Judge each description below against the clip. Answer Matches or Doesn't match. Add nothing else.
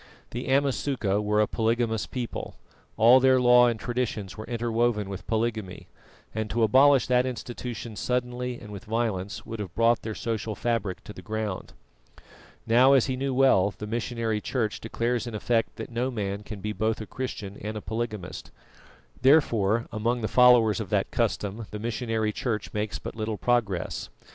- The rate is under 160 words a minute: Doesn't match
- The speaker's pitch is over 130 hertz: Doesn't match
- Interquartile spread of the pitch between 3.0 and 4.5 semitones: Doesn't match